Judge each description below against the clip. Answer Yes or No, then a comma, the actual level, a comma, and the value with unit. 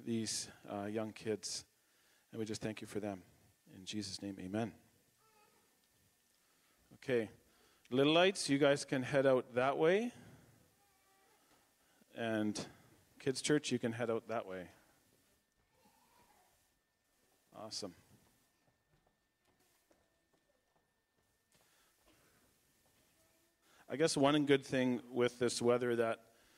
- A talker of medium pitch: No, low, 120 Hz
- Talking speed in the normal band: No, slow, 100 wpm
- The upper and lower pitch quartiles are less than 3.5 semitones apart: No, average, 4.2 semitones